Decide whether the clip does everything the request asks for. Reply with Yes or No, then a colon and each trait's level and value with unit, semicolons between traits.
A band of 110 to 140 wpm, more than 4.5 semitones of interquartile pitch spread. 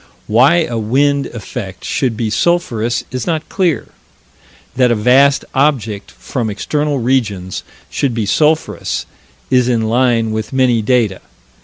No: slow, 135 wpm; average, 4.1 semitones